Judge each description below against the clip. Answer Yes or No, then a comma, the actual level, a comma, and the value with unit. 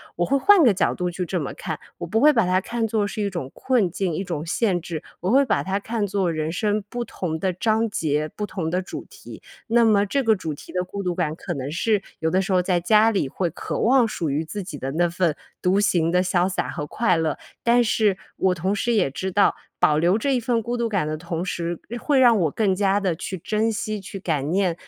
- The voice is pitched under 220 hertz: Yes, high, 190 Hz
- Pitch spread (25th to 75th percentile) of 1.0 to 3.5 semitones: No, average, 4.2 semitones